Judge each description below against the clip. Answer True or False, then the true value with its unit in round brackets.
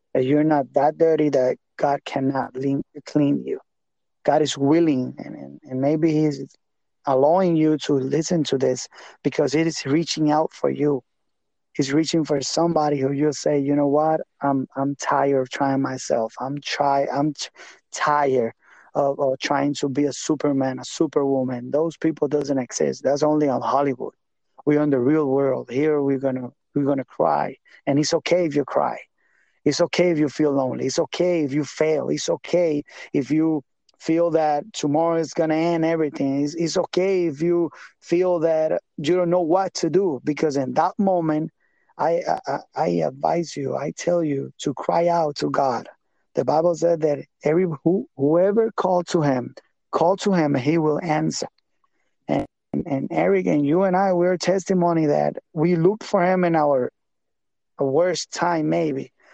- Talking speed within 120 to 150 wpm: False (175 wpm)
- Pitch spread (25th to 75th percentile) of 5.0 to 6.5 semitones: False (3.2 semitones)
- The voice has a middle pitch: True (150 Hz)